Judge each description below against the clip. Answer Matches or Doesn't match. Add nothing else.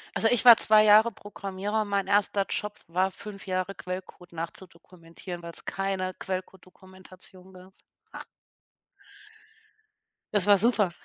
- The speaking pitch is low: Doesn't match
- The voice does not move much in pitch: Matches